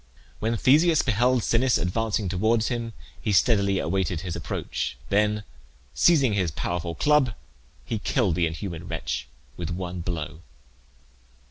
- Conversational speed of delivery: No, slow, 130 wpm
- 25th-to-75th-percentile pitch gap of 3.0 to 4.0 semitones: No, average, 5.1 semitones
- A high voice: No, low, 100 Hz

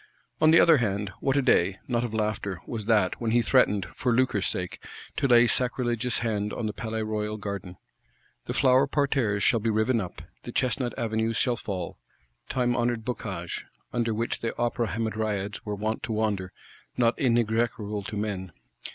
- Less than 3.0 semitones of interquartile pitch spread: Yes, narrow, 2.6 semitones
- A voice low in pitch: Yes, low, 110 Hz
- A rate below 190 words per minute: Yes, average, 175 wpm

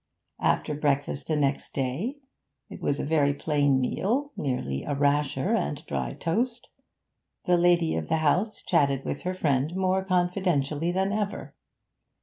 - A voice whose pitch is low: No, medium, 160 Hz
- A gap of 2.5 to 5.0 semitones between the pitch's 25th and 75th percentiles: Yes, average, 4.7 semitones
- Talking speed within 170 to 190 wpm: No, average, 145 wpm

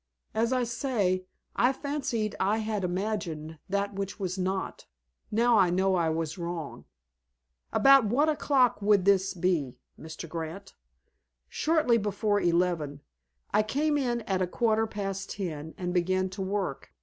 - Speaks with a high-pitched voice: Yes, high, 195 Hz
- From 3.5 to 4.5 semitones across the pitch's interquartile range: Yes, average, 3.9 semitones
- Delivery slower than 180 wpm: Yes, average, 145 wpm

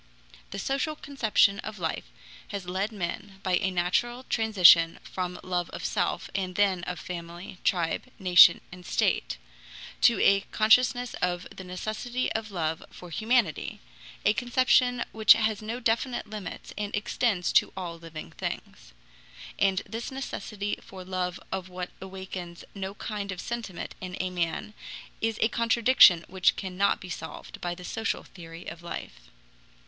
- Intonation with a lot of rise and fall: No, average, 3.7 semitones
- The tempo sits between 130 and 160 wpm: Yes, average, 150 wpm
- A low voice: No, high, 190 Hz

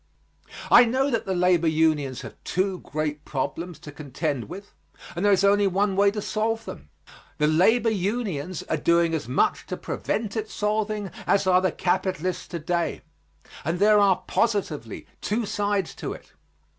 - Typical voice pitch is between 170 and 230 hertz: Yes, medium, 185 Hz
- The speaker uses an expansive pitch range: No, average, 4.5 semitones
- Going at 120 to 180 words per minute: Yes, average, 170 wpm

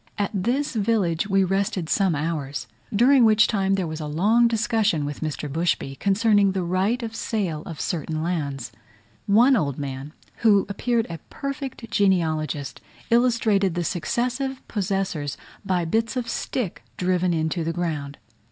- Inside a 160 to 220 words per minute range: No, average, 150 wpm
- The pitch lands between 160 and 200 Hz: Yes, high, 190 Hz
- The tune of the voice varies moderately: No, wide, 5.9 semitones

